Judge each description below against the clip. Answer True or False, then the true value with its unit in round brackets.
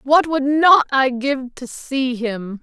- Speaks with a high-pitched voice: True (265 Hz)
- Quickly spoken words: False (185 wpm)